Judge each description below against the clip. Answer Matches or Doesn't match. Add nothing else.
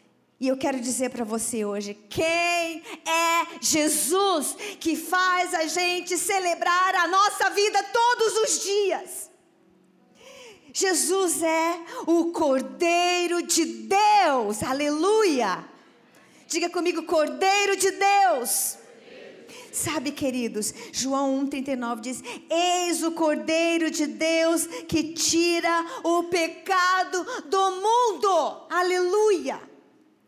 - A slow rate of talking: Matches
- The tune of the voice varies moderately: Matches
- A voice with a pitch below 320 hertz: Doesn't match